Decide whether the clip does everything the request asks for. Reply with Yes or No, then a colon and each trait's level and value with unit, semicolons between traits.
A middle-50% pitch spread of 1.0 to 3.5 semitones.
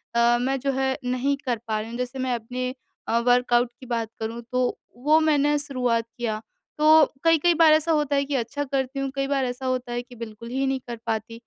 Yes: average, 2.8 semitones